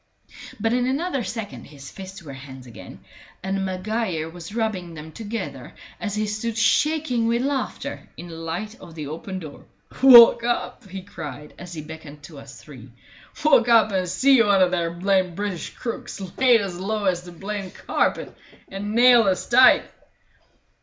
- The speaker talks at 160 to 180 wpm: Yes, average, 170 wpm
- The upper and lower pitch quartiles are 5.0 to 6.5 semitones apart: Yes, wide, 5.5 semitones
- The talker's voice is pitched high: Yes, high, 195 Hz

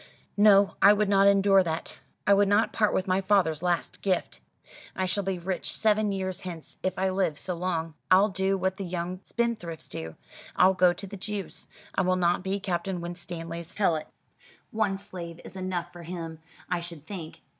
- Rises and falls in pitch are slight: Yes, narrow, 2.3 semitones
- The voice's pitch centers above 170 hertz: Yes, medium, 185 Hz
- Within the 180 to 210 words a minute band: Yes, average, 190 wpm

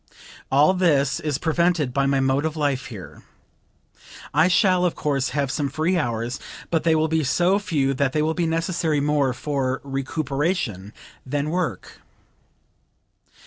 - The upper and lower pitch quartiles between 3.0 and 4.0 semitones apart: Yes, average, 3.4 semitones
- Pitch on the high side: No, medium, 150 Hz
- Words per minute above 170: No, average, 150 wpm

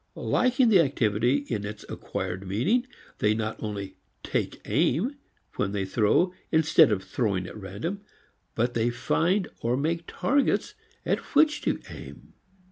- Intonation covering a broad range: Yes, wide, 9.0 semitones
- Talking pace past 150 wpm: No, average, 140 wpm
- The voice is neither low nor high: No, low, 120 Hz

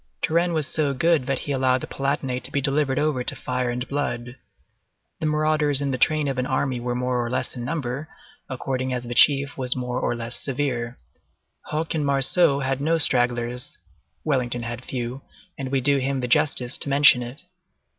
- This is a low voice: Yes, low, 130 Hz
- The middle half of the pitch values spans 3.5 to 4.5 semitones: No, average, 2.7 semitones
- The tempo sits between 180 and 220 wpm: Yes, average, 195 wpm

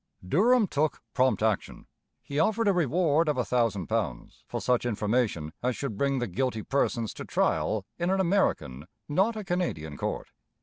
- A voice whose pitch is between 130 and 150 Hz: Yes, low, 135 Hz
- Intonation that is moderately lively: No, wide, 8.3 semitones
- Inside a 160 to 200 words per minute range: Yes, average, 170 wpm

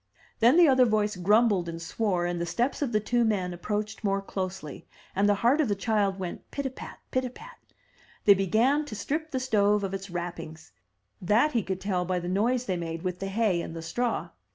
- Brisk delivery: Yes, fast, 225 wpm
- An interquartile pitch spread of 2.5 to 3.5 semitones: No, average, 4.7 semitones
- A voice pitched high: Yes, high, 205 Hz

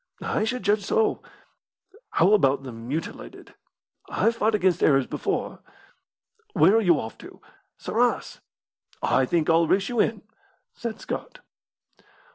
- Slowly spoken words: Yes, slow, 130 wpm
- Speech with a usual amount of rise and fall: No, wide, 6.5 semitones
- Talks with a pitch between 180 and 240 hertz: Yes, high, 190 Hz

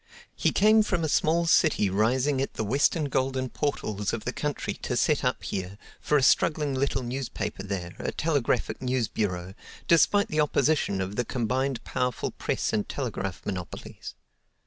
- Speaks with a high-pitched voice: No, low, 130 Hz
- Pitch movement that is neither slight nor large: No, wide, 6.1 semitones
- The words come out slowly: No, average, 165 wpm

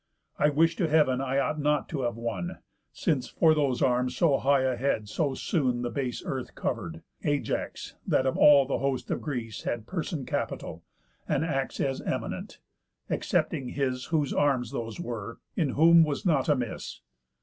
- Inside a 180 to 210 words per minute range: No, average, 170 wpm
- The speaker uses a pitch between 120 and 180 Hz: Yes, low, 135 Hz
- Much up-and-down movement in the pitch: No, average, 3.3 semitones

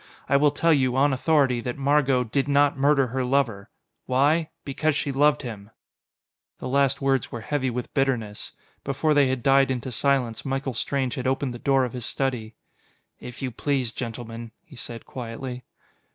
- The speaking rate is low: No, average, 175 wpm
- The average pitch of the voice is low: Yes, low, 130 Hz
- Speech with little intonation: Yes, narrow, 2.3 semitones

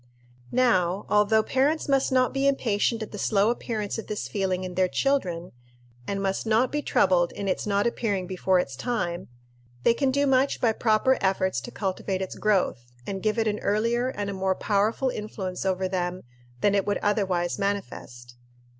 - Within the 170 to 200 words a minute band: Yes, average, 185 wpm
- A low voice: No, high, 205 Hz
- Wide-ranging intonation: No, average, 3.8 semitones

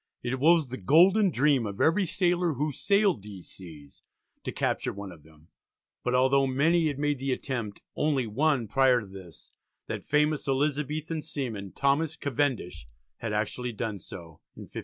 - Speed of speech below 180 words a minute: Yes, average, 165 wpm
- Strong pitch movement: Yes, wide, 6.4 semitones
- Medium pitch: No, low, 130 Hz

